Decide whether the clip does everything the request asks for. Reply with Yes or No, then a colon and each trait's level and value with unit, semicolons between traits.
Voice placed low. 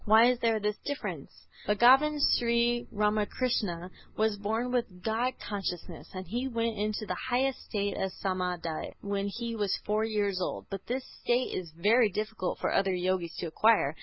No: high, 215 Hz